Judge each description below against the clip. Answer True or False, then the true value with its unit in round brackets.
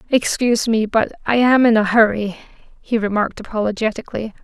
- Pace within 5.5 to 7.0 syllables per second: True (6.1 syllables/s)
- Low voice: False (220 Hz)